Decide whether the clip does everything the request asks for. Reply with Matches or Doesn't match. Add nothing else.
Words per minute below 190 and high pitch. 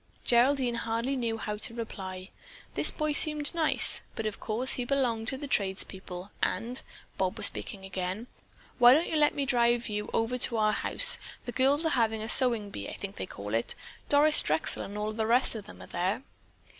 Doesn't match